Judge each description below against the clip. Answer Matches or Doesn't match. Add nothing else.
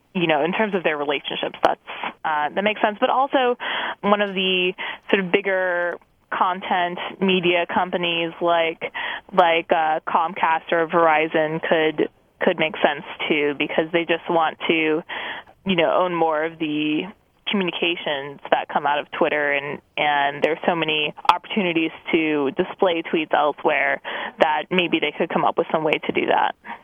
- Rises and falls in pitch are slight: Doesn't match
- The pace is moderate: Matches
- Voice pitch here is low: Doesn't match